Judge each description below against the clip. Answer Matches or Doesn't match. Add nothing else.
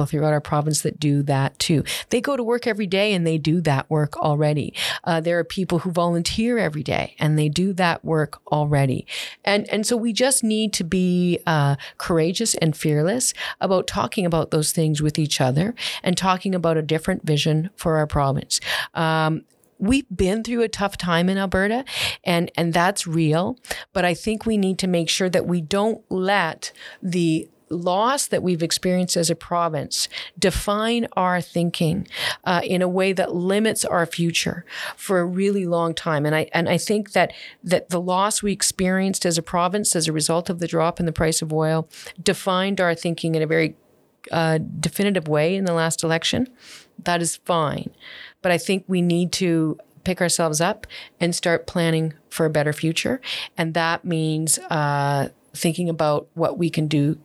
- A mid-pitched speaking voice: Matches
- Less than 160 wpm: Doesn't match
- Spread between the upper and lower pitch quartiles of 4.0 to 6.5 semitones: Doesn't match